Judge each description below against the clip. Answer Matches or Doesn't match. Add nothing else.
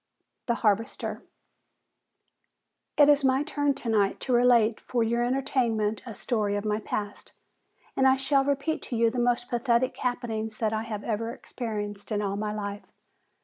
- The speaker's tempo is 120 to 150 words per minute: Doesn't match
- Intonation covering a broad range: Doesn't match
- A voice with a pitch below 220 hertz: Doesn't match